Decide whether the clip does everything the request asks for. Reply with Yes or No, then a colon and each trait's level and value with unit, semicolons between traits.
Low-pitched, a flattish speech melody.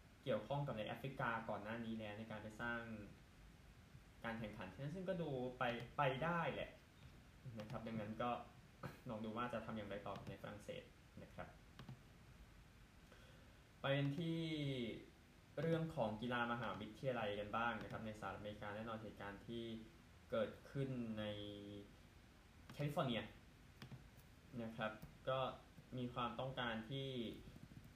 No: low, 115 Hz; average, 3.4 semitones